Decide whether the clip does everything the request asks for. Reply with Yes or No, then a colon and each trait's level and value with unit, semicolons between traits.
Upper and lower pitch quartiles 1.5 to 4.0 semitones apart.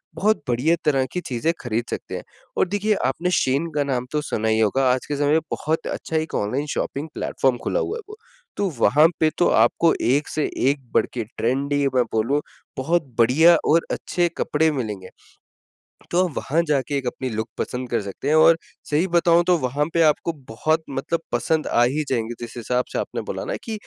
No: average, 4.9 semitones